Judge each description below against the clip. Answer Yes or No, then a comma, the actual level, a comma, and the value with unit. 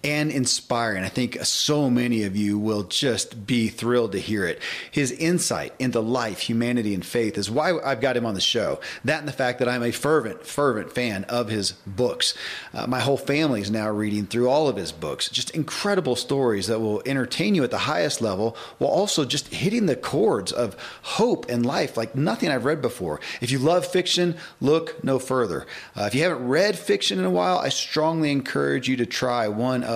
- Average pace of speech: No, fast, 210 wpm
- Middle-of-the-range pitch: No, low, 125 Hz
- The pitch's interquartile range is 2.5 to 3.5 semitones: No, average, 4.6 semitones